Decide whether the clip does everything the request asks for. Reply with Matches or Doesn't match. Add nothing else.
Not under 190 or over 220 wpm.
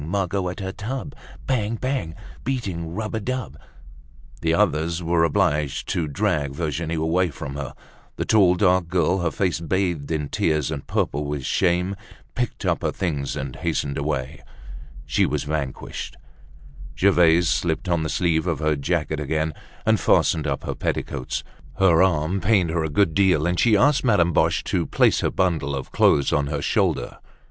Doesn't match